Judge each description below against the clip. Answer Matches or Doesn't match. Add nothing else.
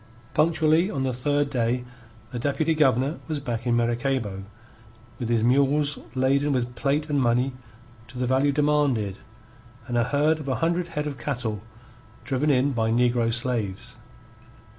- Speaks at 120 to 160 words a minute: Matches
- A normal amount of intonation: Matches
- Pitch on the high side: Doesn't match